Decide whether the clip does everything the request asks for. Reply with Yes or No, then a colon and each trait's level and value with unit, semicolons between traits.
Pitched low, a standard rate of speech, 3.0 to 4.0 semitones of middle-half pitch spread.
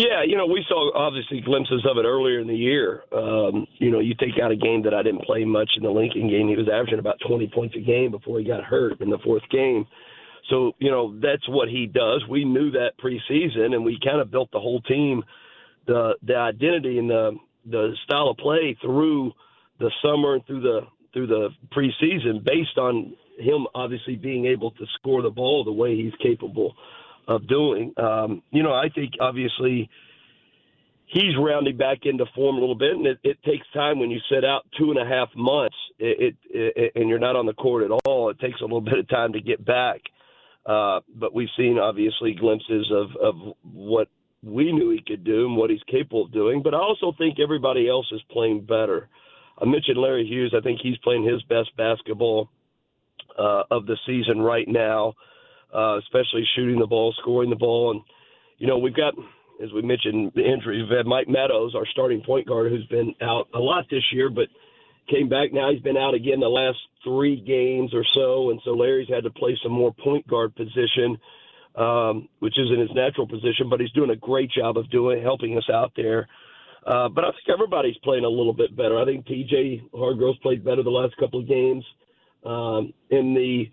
No: low, 125 Hz; fast, 210 wpm; average, 3.5 semitones